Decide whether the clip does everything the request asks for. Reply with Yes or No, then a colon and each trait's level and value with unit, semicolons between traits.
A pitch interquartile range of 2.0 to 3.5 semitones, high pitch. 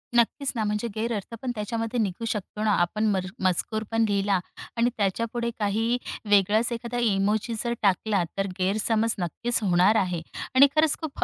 Yes: average, 2.9 semitones; high, 215 Hz